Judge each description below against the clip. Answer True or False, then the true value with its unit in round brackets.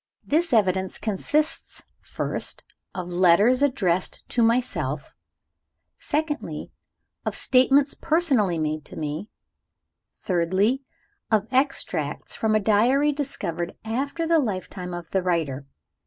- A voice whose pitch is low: False (210 Hz)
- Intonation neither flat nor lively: False (7.7 semitones)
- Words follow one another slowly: True (110 wpm)